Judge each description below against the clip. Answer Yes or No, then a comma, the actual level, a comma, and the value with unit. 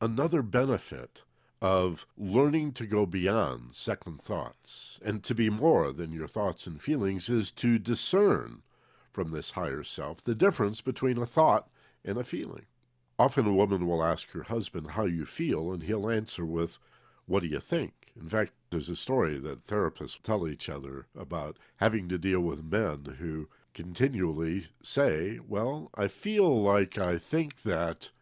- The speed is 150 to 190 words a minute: Yes, average, 165 wpm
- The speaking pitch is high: No, low, 100 Hz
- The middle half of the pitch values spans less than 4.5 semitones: No, wide, 5.6 semitones